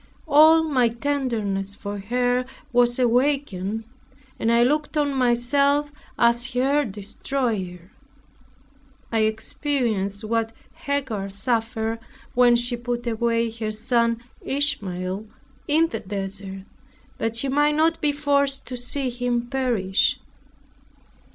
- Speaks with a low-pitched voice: No, high, 240 Hz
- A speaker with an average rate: No, slow, 110 wpm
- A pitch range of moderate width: Yes, average, 4.1 semitones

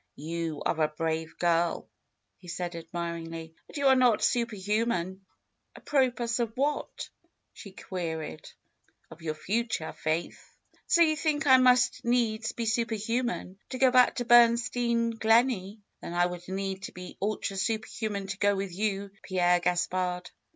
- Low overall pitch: No, high, 200 Hz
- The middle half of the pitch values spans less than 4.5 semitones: No, average, 5.2 semitones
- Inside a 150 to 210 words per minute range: Yes, average, 155 wpm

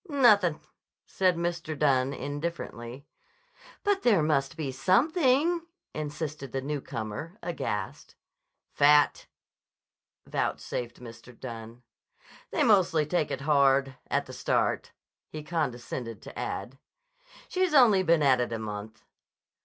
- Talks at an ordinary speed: No, slow, 110 wpm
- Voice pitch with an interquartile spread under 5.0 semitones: No, wide, 5.6 semitones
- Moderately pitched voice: Yes, medium, 150 Hz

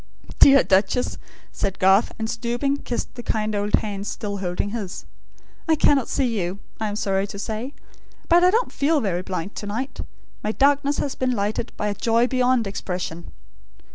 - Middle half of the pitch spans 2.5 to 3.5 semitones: No, average, 4.4 semitones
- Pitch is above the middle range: Yes, high, 220 Hz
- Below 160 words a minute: No, average, 175 wpm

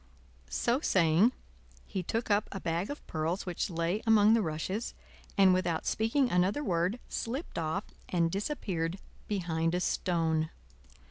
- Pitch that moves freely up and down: No, average, 4.5 semitones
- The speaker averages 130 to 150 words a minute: Yes, average, 140 wpm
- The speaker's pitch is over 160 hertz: Yes, medium, 185 Hz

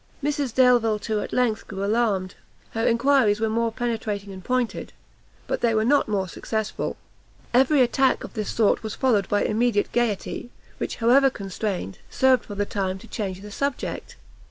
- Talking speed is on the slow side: No, average, 170 wpm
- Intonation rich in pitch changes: No, average, 3.3 semitones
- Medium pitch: No, high, 225 Hz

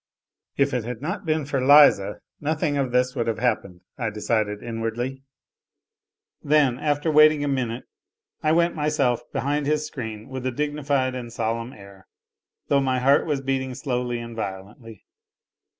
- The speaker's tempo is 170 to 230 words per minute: No, average, 155 wpm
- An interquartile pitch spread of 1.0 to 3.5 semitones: No, average, 4.0 semitones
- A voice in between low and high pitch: No, low, 130 Hz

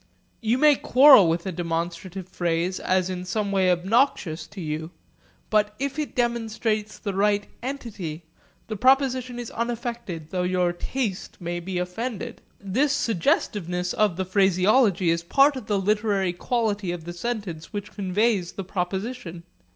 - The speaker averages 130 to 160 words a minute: Yes, average, 150 wpm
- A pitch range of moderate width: Yes, average, 4.7 semitones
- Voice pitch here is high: Yes, high, 195 Hz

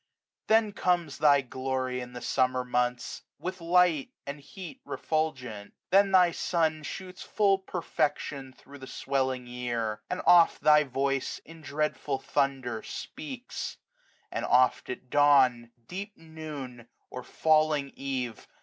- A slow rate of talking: Yes, slow, 130 wpm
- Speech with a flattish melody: No, average, 4.8 semitones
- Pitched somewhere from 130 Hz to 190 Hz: Yes, medium, 140 Hz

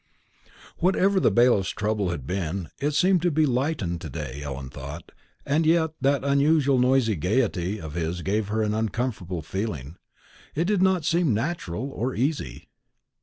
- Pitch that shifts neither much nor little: No, wide, 9.0 semitones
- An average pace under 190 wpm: Yes, average, 160 wpm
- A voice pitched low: Yes, low, 115 Hz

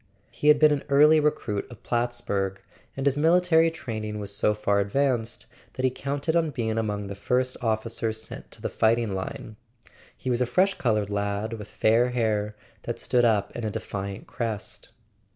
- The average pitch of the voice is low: Yes, low, 115 Hz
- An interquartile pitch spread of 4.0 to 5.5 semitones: Yes, average, 4.5 semitones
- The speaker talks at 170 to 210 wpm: Yes, average, 180 wpm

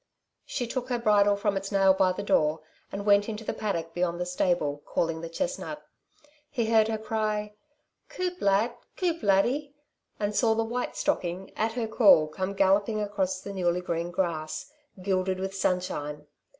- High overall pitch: Yes, high, 200 Hz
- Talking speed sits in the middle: Yes, average, 170 wpm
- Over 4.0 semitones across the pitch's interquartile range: No, average, 3.5 semitones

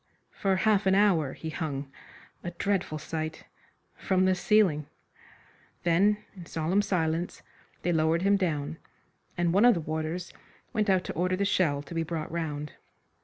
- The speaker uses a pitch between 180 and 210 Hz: No, medium, 170 Hz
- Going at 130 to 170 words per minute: Yes, average, 160 wpm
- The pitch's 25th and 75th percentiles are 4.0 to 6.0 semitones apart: No, average, 3.4 semitones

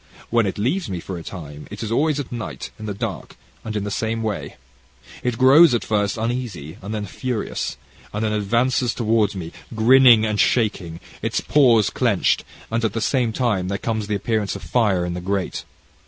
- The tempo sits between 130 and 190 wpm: No, average, 200 wpm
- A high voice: No, low, 110 Hz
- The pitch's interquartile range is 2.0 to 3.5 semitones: Yes, average, 3.1 semitones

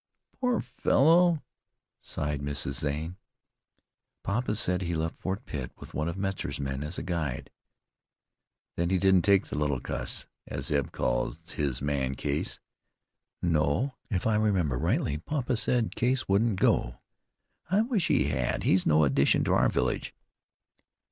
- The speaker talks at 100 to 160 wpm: Yes, average, 150 wpm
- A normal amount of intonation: No, wide, 6.9 semitones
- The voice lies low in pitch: Yes, very low, 85 Hz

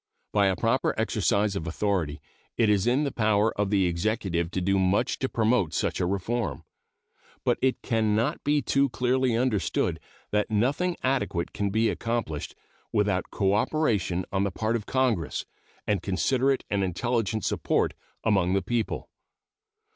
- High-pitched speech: No, low, 105 Hz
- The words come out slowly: No, average, 155 wpm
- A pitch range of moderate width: Yes, average, 3.8 semitones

